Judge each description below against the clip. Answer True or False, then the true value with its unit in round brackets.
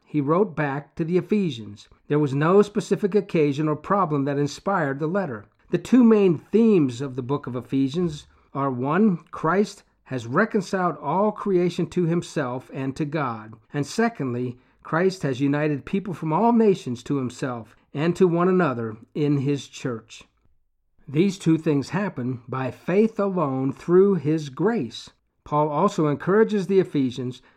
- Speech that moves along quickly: False (155 wpm)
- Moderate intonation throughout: False (5.7 semitones)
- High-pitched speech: False (155 Hz)